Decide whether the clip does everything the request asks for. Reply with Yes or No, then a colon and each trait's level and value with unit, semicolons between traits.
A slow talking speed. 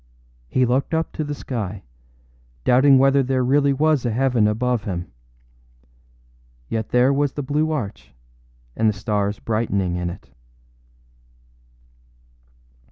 Yes: slow, 125 wpm